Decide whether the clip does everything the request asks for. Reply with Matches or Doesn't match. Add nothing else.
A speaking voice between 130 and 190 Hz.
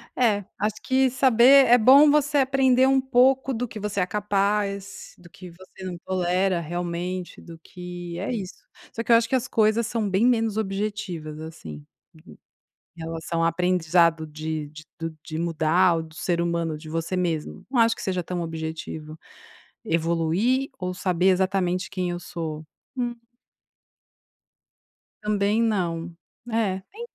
Matches